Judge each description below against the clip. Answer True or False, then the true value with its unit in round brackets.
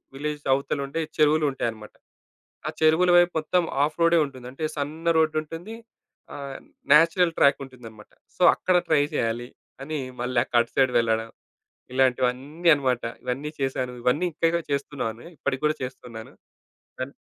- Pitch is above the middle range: False (140 Hz)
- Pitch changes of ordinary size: True (3.8 semitones)